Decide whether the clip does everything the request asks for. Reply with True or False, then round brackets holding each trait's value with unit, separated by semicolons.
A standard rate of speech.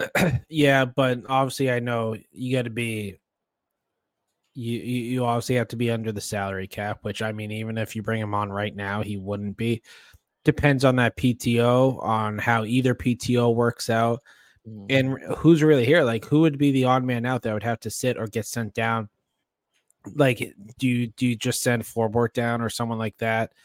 True (195 wpm)